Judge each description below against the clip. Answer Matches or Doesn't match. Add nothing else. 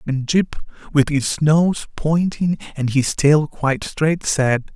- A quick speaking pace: Doesn't match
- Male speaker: Matches